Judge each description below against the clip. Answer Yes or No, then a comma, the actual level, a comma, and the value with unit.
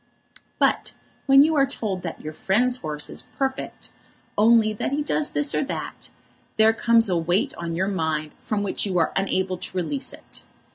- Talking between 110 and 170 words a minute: No, average, 185 wpm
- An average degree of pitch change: No, wide, 6.2 semitones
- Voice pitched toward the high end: Yes, high, 205 Hz